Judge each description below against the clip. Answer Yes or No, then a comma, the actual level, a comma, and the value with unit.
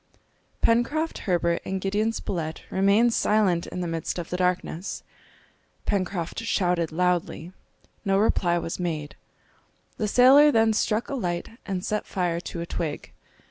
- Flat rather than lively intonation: No, average, 3.9 semitones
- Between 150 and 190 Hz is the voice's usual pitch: Yes, medium, 185 Hz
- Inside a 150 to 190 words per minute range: No, average, 140 wpm